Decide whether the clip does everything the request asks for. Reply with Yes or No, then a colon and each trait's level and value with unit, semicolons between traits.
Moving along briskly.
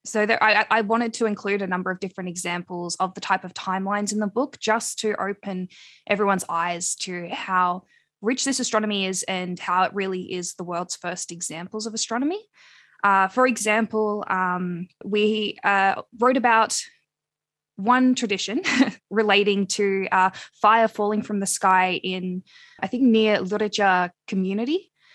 No: average, 155 wpm